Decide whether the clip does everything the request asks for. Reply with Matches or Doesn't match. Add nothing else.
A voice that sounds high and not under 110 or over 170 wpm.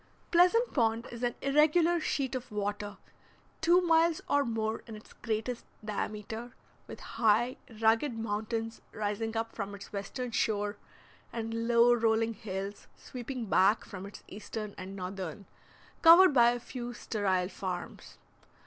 Matches